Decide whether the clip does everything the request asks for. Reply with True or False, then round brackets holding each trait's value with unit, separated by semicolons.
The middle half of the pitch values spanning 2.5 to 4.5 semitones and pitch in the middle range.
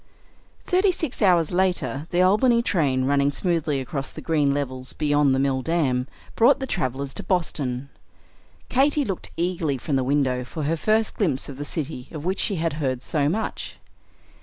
False (5.2 semitones; 150 Hz)